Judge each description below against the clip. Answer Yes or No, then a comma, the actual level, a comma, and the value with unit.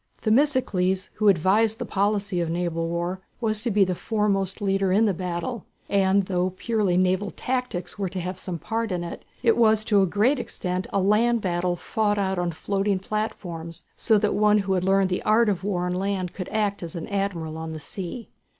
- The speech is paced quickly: Yes, fast, 215 wpm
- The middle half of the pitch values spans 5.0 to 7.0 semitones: No, average, 2.9 semitones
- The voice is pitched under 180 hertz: No, high, 195 Hz